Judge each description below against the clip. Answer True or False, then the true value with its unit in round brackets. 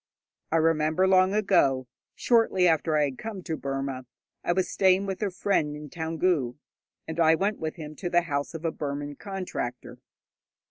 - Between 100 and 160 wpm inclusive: False (175 wpm)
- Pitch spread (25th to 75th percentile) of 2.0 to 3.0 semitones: False (4.2 semitones)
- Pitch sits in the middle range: True (165 Hz)